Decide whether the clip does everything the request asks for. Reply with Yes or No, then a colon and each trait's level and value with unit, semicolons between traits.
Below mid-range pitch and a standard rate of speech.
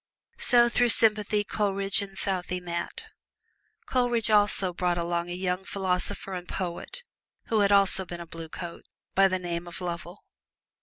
No: high, 190 Hz; average, 155 wpm